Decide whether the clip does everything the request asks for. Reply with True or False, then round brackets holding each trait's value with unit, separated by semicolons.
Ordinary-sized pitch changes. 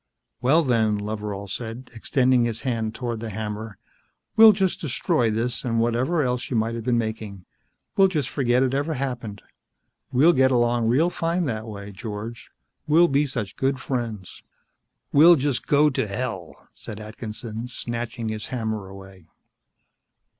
True (3.4 semitones)